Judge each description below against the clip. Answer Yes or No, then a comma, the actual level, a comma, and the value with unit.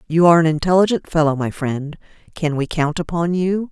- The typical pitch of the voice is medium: Yes, medium, 165 Hz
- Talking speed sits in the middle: Yes, average, 195 wpm